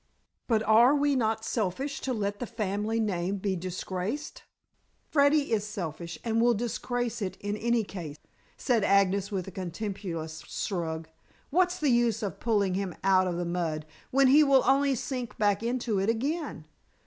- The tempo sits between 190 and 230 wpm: No, average, 165 wpm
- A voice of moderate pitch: No, high, 215 Hz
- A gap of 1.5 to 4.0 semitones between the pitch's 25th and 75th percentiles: No, average, 4.6 semitones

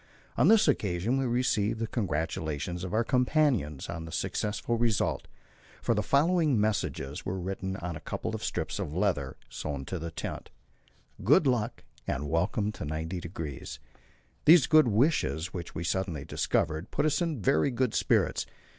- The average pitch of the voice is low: Yes, low, 100 Hz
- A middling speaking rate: Yes, average, 160 wpm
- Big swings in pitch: Yes, wide, 7.4 semitones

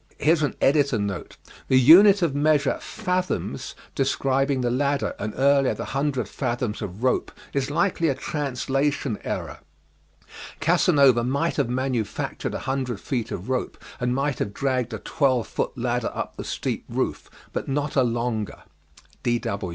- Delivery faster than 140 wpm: No, slow, 135 wpm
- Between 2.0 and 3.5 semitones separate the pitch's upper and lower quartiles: Yes, average, 2.8 semitones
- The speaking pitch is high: No, low, 135 Hz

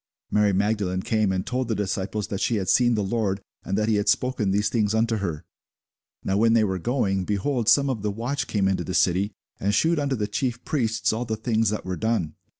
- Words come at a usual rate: No, fast, 230 wpm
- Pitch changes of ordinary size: Yes, average, 3.1 semitones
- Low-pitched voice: Yes, low, 105 Hz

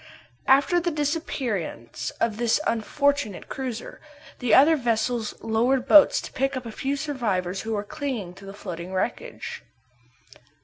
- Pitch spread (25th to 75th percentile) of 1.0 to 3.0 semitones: No, average, 5.1 semitones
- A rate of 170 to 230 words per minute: No, average, 140 wpm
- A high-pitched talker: Yes, high, 240 Hz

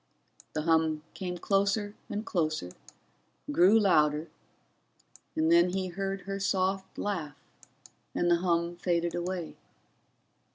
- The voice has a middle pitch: Yes, medium, 175 Hz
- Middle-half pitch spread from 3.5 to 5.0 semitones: No, average, 3.0 semitones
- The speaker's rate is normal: No, slow, 115 wpm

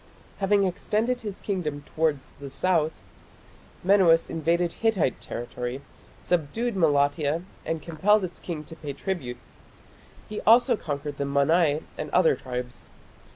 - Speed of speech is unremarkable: No, slow, 125 wpm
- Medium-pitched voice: Yes, medium, 165 Hz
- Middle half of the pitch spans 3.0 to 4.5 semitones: No, average, 5.1 semitones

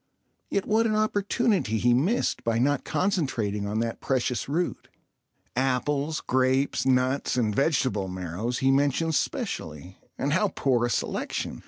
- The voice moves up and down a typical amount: No, wide, 5.8 semitones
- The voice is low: Yes, low, 130 Hz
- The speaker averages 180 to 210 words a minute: No, slow, 135 wpm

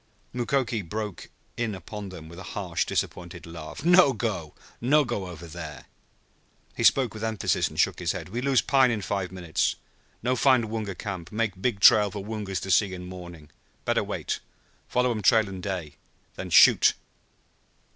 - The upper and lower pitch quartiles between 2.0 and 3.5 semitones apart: No, average, 4.3 semitones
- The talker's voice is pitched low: Yes, low, 100 Hz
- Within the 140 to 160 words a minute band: No, average, 175 wpm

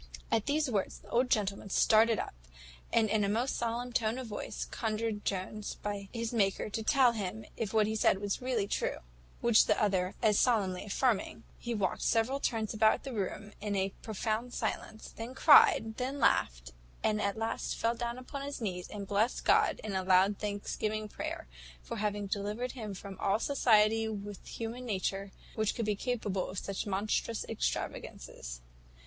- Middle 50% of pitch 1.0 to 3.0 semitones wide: Yes, narrow, 2.6 semitones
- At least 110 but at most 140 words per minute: No, average, 180 wpm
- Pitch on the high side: Yes, high, 215 Hz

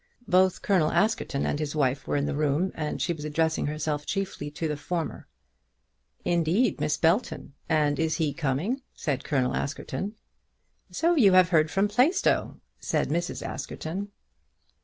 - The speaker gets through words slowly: No, average, 155 wpm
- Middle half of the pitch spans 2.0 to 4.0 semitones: No, average, 4.4 semitones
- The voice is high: No, medium, 160 Hz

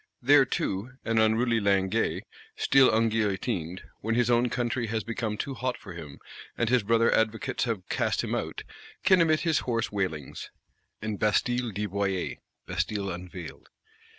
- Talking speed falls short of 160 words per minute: Yes, average, 150 wpm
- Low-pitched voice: Yes, low, 110 Hz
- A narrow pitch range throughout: No, average, 3.7 semitones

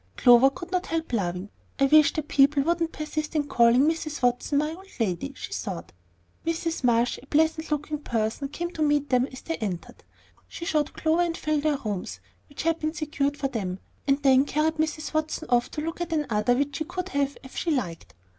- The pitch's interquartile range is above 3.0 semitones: Yes, average, 4.2 semitones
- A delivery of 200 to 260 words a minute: Yes, fast, 205 wpm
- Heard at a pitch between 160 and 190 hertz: No, very high, 290 Hz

